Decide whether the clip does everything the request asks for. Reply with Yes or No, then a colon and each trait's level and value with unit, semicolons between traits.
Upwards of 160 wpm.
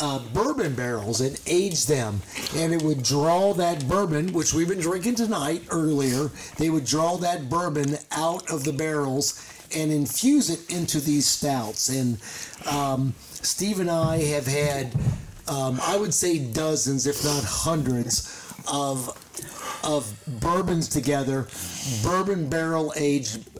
No: average, 140 wpm